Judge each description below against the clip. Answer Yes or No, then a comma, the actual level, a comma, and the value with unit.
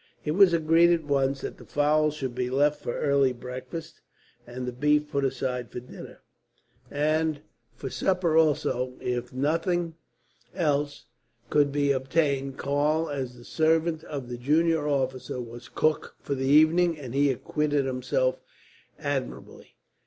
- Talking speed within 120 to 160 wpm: Yes, average, 145 wpm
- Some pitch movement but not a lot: Yes, average, 3.2 semitones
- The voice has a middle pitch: Yes, medium, 145 Hz